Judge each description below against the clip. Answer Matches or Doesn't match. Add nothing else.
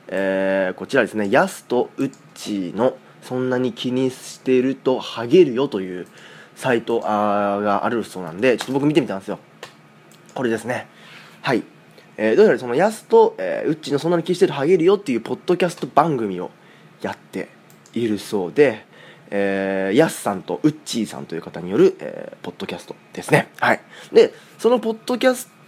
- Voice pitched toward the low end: Matches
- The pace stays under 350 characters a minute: Doesn't match